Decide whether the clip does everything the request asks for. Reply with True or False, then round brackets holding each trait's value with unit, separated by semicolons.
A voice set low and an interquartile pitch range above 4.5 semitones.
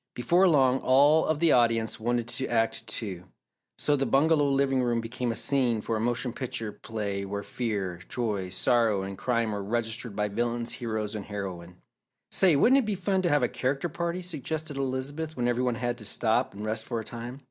False (120 Hz; 4.1 semitones)